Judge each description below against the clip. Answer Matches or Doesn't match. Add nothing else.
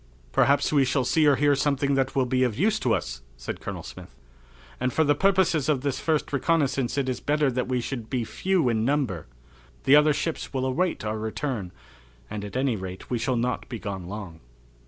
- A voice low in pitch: Matches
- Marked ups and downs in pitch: Doesn't match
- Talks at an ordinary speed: Doesn't match